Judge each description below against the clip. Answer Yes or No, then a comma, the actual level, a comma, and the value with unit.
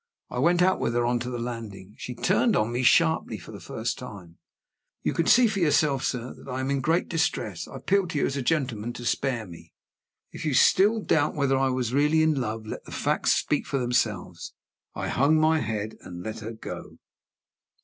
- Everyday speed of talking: No, fast, 215 wpm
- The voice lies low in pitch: Yes, low, 130 Hz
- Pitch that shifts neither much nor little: No, wide, 5.8 semitones